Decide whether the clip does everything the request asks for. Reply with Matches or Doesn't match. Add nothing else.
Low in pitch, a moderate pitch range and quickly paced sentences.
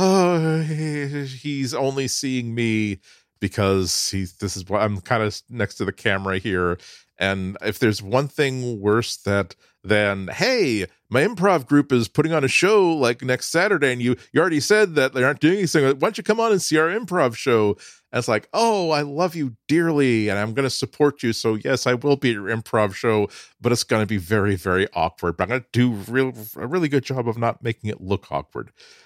Doesn't match